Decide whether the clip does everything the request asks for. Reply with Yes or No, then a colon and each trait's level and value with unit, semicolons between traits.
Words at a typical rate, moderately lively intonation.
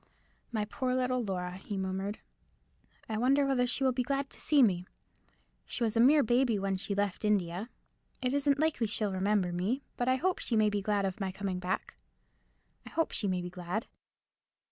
Yes: average, 190 wpm; average, 4.9 semitones